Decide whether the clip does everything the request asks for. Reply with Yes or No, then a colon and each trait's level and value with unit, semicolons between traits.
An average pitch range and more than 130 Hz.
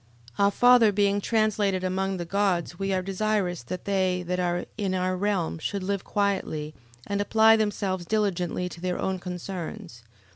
No: narrow, 2.2 semitones; high, 190 Hz